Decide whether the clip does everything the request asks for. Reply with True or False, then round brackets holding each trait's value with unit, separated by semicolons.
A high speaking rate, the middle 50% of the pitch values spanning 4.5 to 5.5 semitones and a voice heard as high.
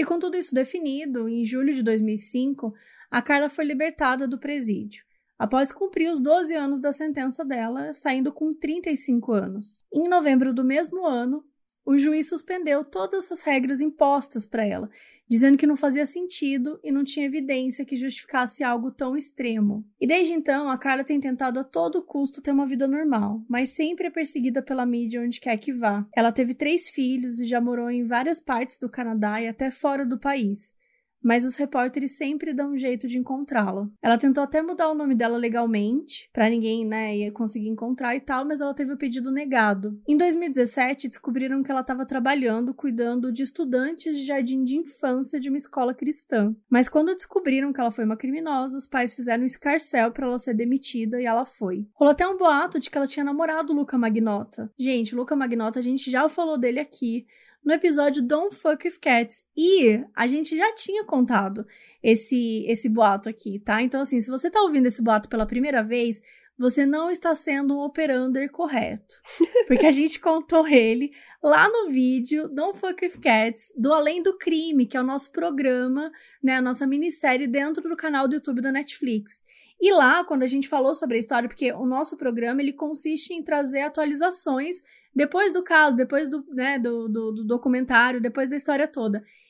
False (190 wpm; 3.8 semitones; 270 Hz)